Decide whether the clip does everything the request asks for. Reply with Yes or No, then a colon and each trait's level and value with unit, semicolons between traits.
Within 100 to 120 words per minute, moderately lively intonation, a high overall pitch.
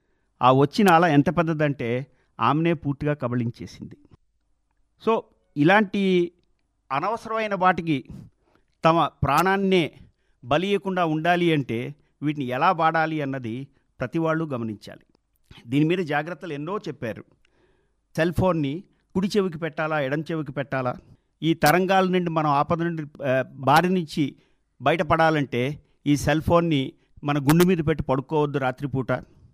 No: average, 110 wpm; average, 3.8 semitones; medium, 155 Hz